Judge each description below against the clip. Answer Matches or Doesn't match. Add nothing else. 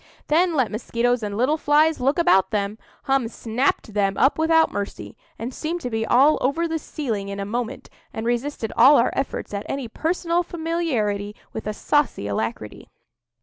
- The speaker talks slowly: Doesn't match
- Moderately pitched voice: Doesn't match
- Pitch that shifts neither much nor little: Doesn't match